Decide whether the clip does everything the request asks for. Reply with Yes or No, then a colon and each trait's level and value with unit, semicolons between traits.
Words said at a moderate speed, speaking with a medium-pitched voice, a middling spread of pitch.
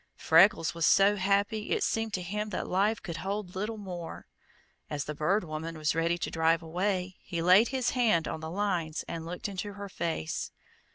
Yes: average, 190 wpm; medium, 180 Hz; average, 3.7 semitones